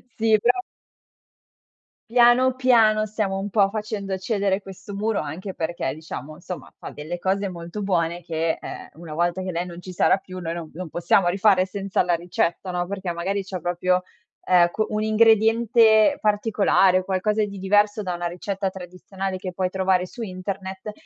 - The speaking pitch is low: No, high, 190 Hz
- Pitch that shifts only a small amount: No, average, 3.0 semitones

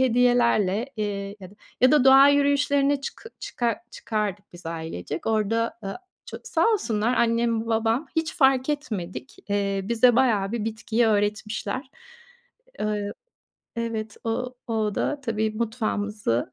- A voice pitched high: Yes, high, 225 Hz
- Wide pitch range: No, average, 3.4 semitones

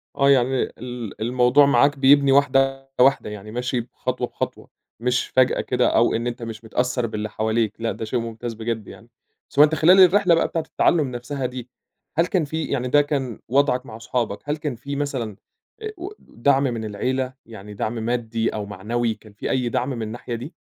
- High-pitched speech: No, low, 125 Hz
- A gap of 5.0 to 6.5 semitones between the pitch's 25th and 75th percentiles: No, average, 3.4 semitones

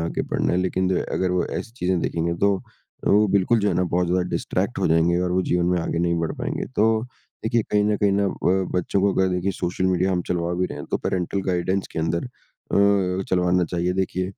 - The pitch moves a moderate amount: No, narrow, 1.6 semitones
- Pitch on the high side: No, very low, 90 Hz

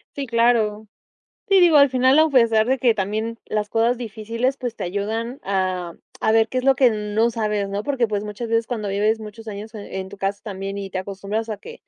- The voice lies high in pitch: Yes, high, 220 Hz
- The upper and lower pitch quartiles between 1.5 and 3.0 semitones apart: Yes, average, 2.7 semitones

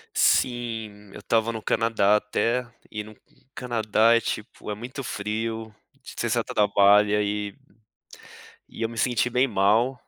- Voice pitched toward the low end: Yes, low, 110 Hz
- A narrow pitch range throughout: Yes, narrow, 2.0 semitones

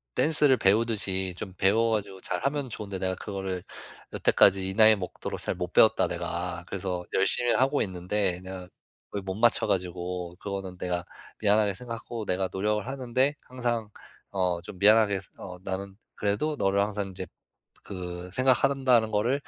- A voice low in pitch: Yes, low, 100 Hz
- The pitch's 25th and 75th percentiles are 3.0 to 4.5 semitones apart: Yes, average, 3.7 semitones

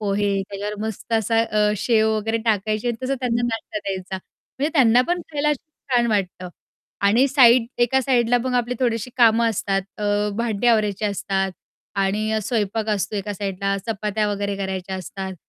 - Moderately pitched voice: No, high, 215 Hz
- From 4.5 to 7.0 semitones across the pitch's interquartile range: No, average, 3.1 semitones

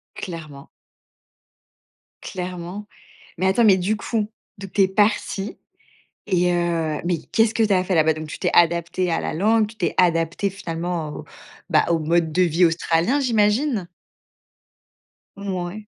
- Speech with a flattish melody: No, average, 3.7 semitones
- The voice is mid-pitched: Yes, medium, 180 Hz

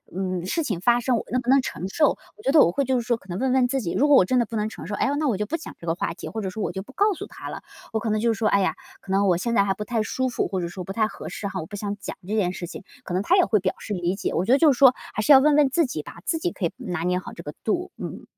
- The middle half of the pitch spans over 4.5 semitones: Yes, wide, 5.6 semitones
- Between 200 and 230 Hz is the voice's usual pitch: Yes, high, 215 Hz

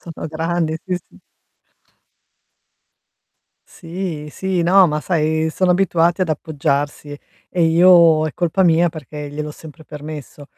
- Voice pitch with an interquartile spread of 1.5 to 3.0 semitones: Yes, narrow, 2.5 semitones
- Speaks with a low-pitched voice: No, medium, 160 Hz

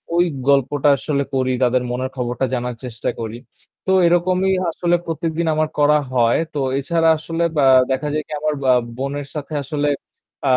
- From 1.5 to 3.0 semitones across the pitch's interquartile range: No, average, 4.1 semitones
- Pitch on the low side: No, medium, 145 Hz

